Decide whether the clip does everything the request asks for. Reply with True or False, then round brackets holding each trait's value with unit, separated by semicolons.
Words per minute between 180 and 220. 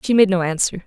False (280 wpm)